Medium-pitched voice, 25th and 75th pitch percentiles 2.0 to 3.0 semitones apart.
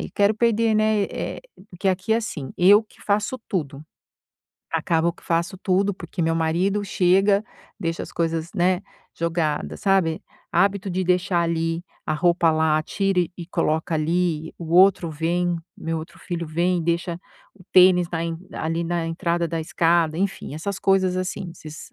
Yes: medium, 175 Hz; narrow, 2.6 semitones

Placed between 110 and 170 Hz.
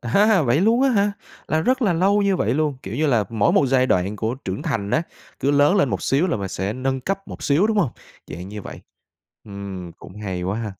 Yes: low, 135 Hz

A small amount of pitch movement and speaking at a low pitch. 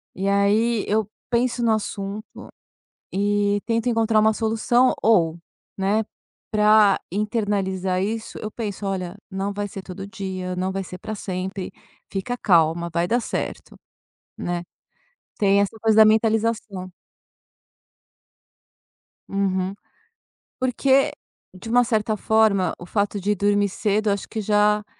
No: narrow, 2.3 semitones; high, 205 Hz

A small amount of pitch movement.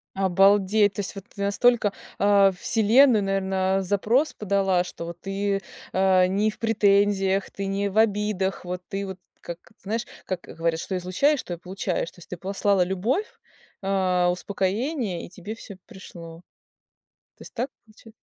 Yes: narrow, 2.0 semitones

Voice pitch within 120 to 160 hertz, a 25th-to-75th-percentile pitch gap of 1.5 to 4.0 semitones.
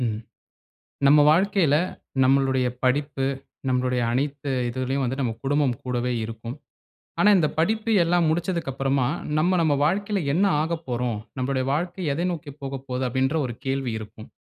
No: low, 135 Hz; average, 4.4 semitones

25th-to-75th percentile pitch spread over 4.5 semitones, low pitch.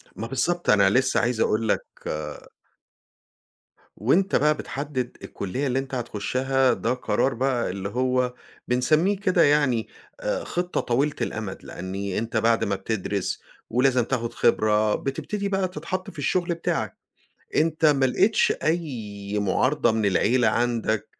Yes: wide, 5.5 semitones; low, 125 Hz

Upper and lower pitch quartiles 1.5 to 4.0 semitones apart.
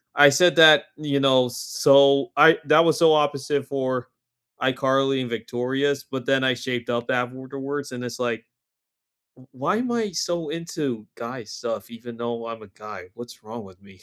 Yes: average, 3.2 semitones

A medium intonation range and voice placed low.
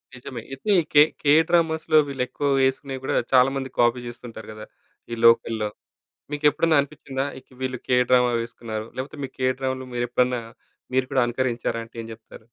No: narrow, 2.2 semitones; low, 130 Hz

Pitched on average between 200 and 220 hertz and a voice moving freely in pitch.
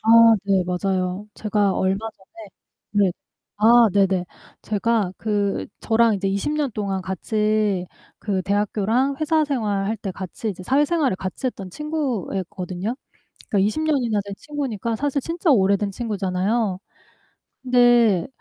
No: high, 210 Hz; average, 3.9 semitones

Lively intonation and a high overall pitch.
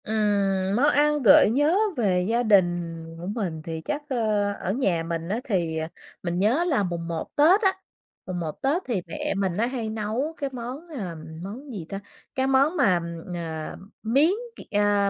Yes: wide, 7.3 semitones; high, 215 Hz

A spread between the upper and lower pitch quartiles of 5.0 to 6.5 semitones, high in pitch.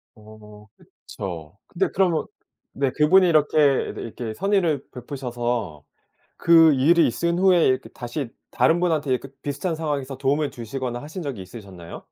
No: wide, 5.4 semitones; low, 135 Hz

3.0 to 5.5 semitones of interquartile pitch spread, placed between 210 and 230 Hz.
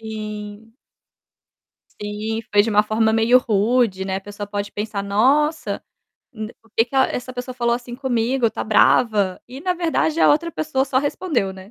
Yes: average, 3.8 semitones; high, 225 Hz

